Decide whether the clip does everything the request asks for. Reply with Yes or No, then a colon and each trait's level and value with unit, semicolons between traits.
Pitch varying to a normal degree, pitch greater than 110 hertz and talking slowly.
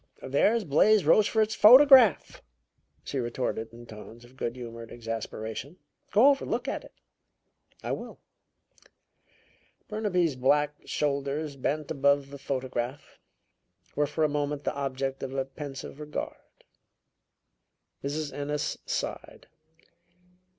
Yes: average, 3.1 semitones; medium, 140 Hz; slow, 115 wpm